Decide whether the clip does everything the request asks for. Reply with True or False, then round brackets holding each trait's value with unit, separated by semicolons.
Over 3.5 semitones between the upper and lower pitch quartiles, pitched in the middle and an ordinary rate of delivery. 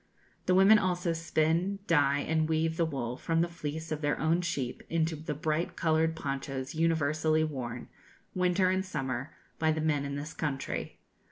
False (2.6 semitones; 160 Hz; 170 wpm)